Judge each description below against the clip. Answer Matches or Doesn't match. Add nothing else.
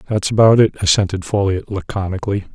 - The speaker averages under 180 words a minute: Matches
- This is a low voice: Matches